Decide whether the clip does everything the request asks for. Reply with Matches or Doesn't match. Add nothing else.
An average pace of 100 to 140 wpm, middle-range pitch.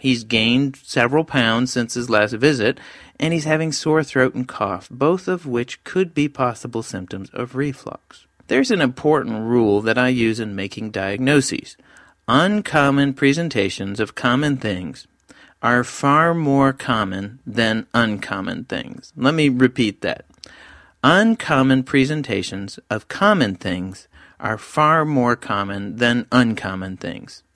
Doesn't match